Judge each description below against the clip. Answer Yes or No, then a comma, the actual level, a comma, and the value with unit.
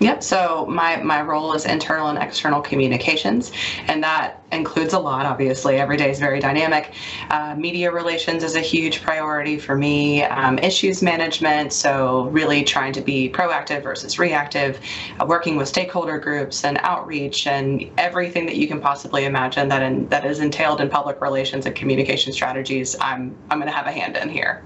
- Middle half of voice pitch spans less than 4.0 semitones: Yes, average, 2.8 semitones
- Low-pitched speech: No, medium, 145 Hz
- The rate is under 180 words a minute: No, average, 185 wpm